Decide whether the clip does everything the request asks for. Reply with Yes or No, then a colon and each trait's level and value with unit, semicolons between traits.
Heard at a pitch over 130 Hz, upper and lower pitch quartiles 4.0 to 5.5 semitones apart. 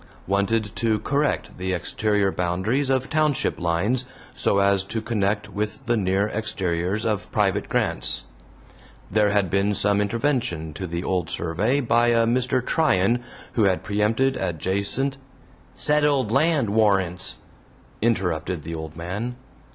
No: low, 105 Hz; average, 4.3 semitones